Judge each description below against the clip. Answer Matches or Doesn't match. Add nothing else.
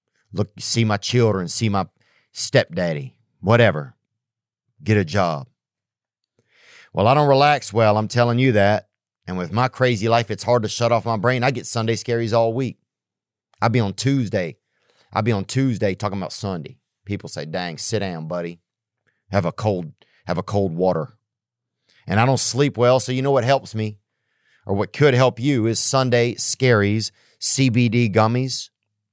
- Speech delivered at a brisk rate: Doesn't match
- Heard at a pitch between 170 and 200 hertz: Doesn't match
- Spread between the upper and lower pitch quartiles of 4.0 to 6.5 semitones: Doesn't match